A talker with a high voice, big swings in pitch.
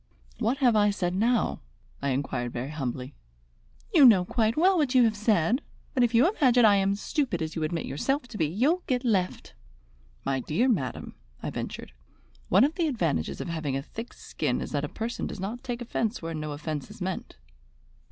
Yes: high, 210 Hz; wide, 7.9 semitones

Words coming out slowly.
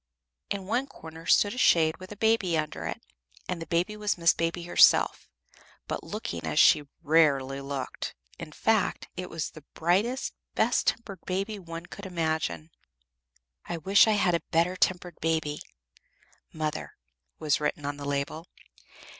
No: average, 160 wpm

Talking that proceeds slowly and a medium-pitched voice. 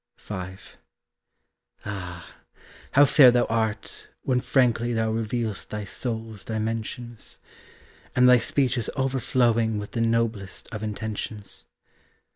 No: slow, 110 wpm; low, 115 Hz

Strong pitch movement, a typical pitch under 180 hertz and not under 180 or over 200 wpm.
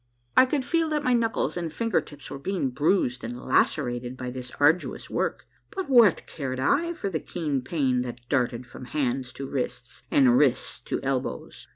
Yes: wide, 7.7 semitones; medium, 140 Hz; average, 185 wpm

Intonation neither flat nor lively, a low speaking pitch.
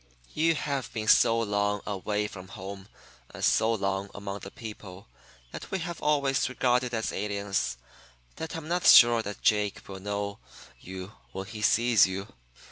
Yes: average, 3.7 semitones; low, 105 Hz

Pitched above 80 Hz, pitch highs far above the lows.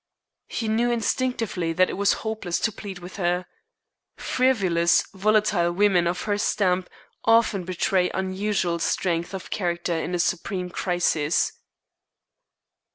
No: medium, 185 Hz; average, 3.3 semitones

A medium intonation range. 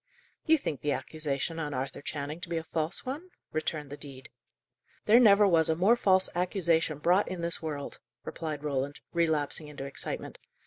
Yes: average, 3.7 semitones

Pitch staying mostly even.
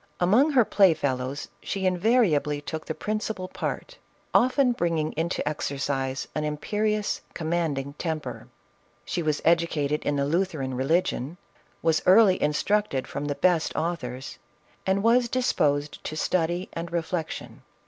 No: average, 4.6 semitones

